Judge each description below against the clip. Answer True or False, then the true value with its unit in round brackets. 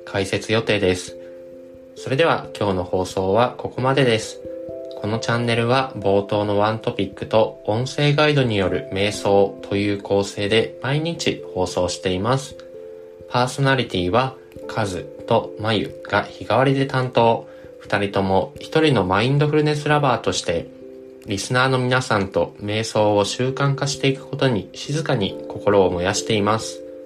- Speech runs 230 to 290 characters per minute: False (315 characters per minute)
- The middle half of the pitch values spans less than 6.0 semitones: True (5.5 semitones)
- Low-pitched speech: True (110 Hz)